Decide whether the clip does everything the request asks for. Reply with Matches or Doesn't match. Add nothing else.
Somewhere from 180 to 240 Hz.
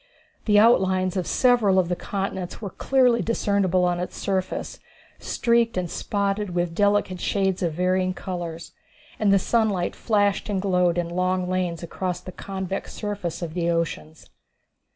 Matches